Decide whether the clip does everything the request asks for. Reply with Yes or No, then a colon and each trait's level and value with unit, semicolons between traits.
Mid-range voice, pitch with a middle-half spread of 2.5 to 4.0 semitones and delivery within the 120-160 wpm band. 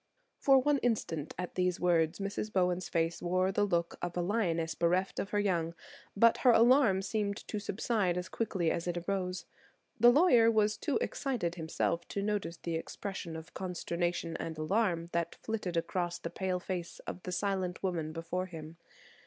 No: medium, 180 Hz; average, 3.4 semitones; average, 175 wpm